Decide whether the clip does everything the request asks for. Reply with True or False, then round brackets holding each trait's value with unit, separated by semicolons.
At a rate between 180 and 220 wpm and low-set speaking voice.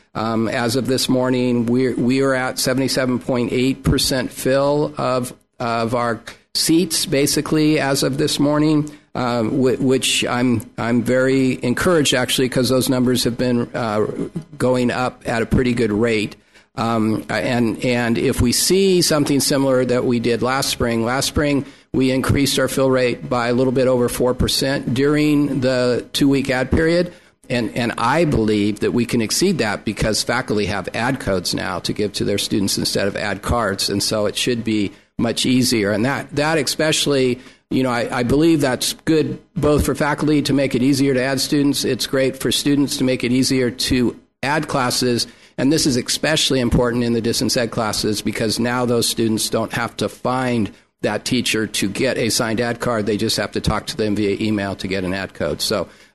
True (190 wpm; 125 Hz)